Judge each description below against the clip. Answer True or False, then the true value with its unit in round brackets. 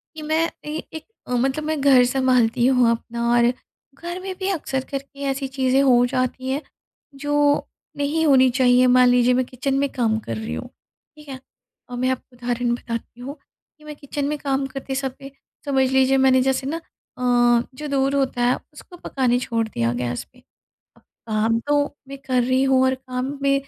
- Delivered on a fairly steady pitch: True (2.1 semitones)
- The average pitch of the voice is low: False (260 Hz)